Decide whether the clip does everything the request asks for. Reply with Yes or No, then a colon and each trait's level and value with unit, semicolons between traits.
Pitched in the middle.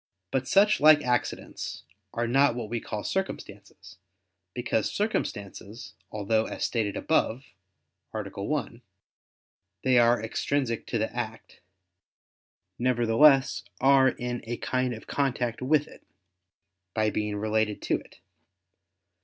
No: low, 120 Hz